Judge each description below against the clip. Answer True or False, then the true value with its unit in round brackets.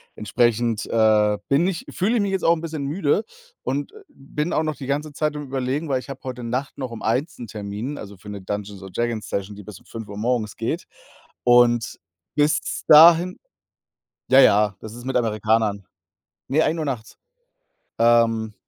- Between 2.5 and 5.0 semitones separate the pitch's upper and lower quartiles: False (5.4 semitones)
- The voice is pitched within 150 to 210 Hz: False (120 Hz)